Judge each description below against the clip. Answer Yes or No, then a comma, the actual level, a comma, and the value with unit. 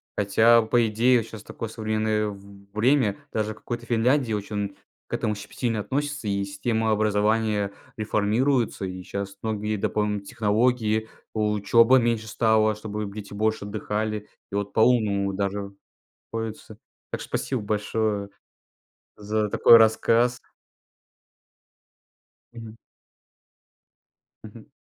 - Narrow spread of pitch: Yes, narrow, 1.7 semitones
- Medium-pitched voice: No, low, 110 Hz